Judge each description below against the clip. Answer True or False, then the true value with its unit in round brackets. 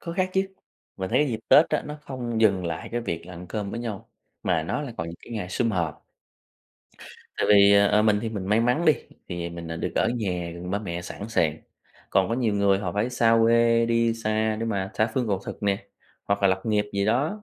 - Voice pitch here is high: False (105 Hz)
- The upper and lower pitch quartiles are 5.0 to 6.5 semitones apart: False (3.7 semitones)